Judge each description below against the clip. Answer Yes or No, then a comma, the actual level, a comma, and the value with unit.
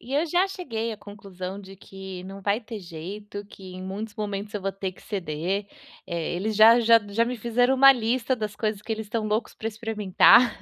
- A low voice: No, high, 210 Hz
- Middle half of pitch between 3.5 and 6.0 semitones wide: No, average, 2.9 semitones